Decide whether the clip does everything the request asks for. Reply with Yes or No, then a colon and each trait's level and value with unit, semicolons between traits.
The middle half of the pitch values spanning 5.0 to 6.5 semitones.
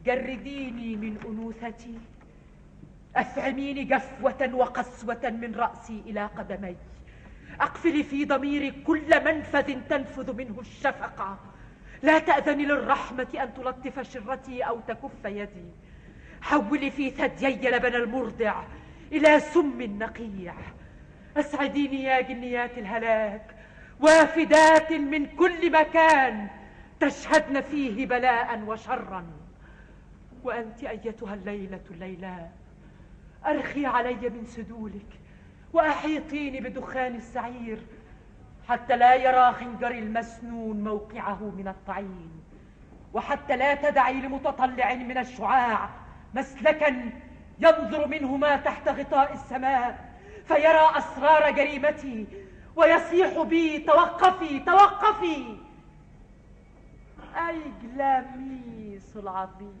No: average, 4.2 semitones